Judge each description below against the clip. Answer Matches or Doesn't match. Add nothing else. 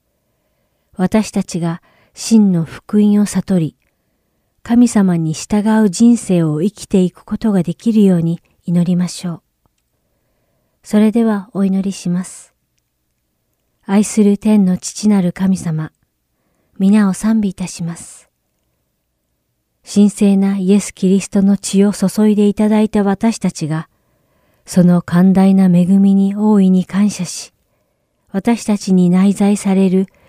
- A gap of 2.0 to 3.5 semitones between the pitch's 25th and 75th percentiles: Matches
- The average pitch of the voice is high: Matches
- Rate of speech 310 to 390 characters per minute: Doesn't match